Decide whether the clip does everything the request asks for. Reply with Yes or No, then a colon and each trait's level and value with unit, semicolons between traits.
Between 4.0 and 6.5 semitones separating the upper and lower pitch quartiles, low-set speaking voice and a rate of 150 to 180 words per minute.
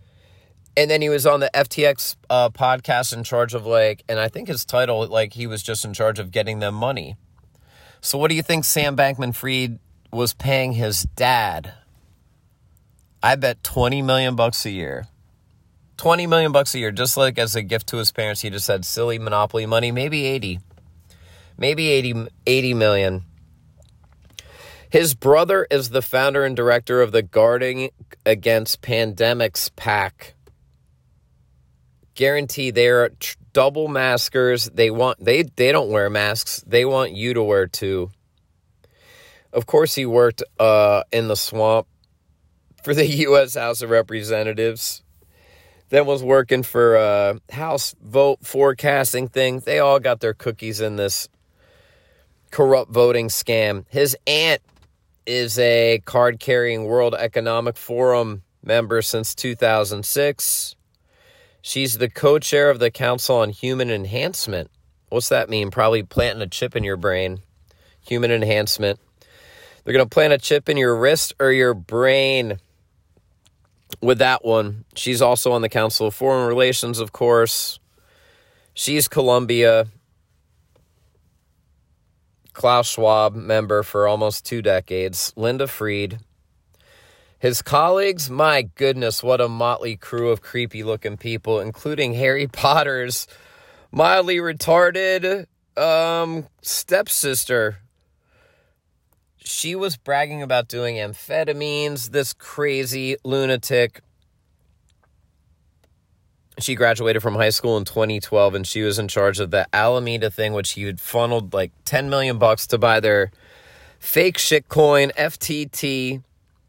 No: average, 4.3 semitones; low, 120 Hz; slow, 135 wpm